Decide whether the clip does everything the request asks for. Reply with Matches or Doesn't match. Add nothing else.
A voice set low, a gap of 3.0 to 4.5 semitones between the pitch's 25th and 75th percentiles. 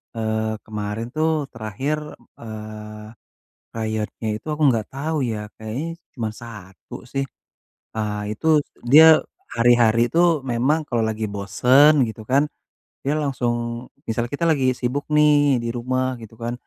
Matches